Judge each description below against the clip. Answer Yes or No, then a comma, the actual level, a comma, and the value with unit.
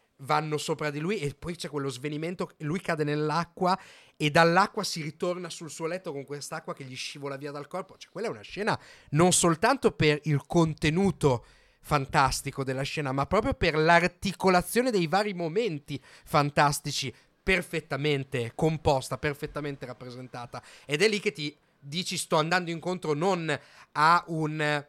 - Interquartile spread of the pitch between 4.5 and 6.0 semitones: No, average, 3.5 semitones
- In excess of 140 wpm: Yes, average, 155 wpm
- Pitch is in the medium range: Yes, medium, 155 Hz